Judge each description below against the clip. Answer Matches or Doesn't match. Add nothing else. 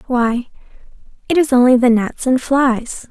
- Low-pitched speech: Doesn't match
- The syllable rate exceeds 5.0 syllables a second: Doesn't match